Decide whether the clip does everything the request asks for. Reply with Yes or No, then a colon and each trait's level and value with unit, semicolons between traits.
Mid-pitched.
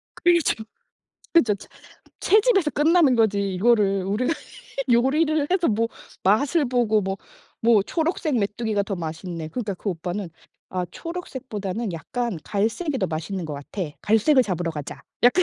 No: high, 220 Hz